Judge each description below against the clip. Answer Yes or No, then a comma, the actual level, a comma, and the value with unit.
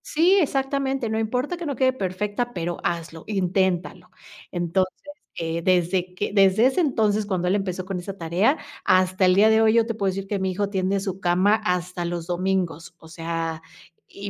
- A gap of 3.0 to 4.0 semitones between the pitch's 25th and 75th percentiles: Yes, average, 3.6 semitones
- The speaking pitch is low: No, high, 190 Hz